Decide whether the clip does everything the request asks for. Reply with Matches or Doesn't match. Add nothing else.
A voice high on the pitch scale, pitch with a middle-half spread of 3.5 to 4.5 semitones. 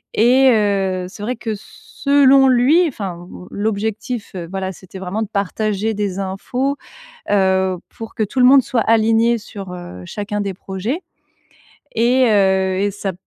Matches